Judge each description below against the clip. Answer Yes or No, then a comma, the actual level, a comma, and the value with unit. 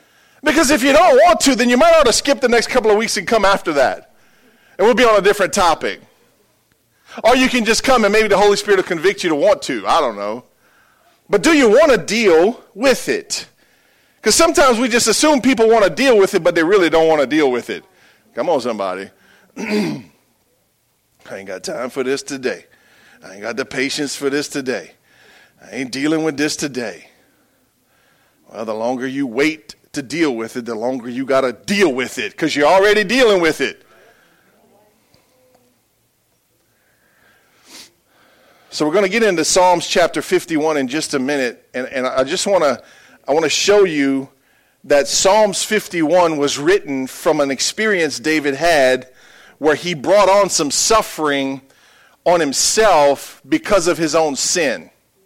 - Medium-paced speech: Yes, average, 180 wpm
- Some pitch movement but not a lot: No, wide, 7.3 semitones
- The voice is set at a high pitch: No, medium, 170 Hz